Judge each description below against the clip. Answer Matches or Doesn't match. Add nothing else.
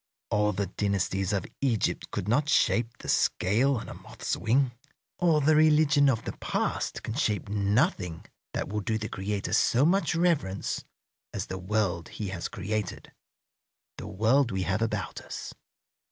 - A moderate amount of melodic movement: Doesn't match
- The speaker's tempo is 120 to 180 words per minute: Matches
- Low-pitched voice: Matches